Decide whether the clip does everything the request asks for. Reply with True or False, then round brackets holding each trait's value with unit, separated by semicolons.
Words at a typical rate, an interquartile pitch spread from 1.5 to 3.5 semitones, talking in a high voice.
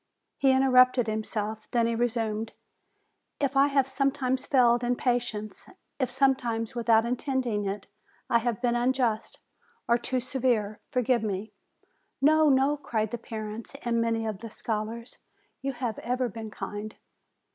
True (145 wpm; 2.8 semitones; 240 Hz)